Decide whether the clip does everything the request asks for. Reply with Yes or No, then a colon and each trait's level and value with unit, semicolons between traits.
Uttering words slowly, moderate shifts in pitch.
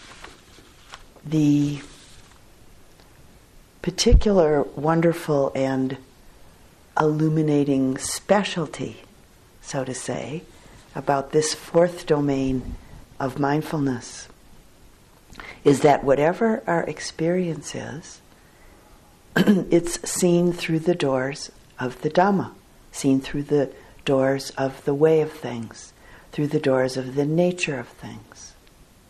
Yes: slow, 95 wpm; average, 3.5 semitones